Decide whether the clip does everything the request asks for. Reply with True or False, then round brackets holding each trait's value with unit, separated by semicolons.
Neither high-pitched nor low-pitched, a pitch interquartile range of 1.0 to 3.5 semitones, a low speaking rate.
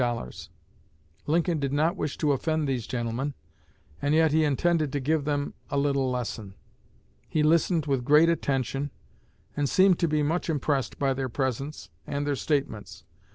False (145 Hz; 2.6 semitones; 155 wpm)